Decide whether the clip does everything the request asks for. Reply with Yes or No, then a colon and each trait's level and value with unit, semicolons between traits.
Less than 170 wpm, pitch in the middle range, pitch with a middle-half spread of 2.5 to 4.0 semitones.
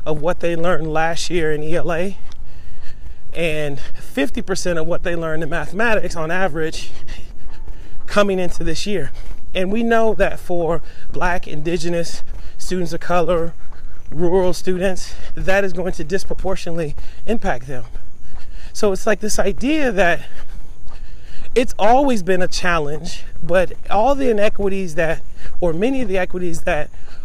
Yes: average, 140 wpm; medium, 175 Hz; average, 3.2 semitones